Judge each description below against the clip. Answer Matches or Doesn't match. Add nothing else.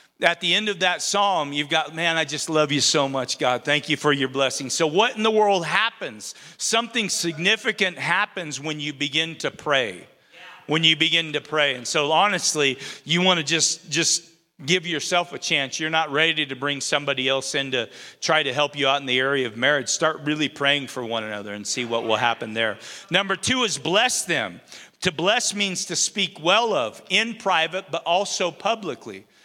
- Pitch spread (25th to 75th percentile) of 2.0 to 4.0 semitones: Doesn't match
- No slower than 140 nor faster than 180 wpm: Doesn't match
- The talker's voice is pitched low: Doesn't match